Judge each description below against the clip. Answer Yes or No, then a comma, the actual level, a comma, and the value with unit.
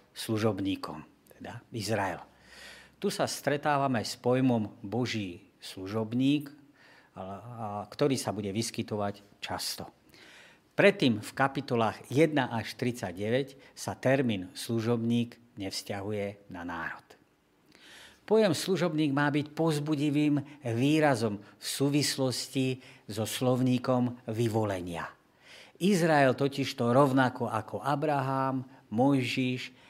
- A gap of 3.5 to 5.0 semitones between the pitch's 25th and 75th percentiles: Yes, average, 4.4 semitones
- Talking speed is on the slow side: Yes, slow, 90 wpm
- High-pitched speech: No, low, 125 Hz